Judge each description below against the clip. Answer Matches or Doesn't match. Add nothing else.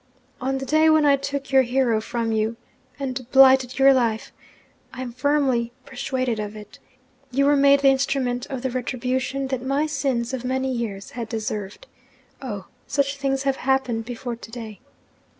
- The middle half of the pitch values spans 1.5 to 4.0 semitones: Matches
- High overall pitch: Matches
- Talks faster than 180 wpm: Doesn't match